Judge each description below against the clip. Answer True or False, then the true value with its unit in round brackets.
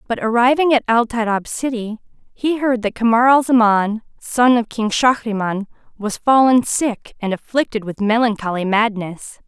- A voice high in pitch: True (230 Hz)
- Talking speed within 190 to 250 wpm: False (150 wpm)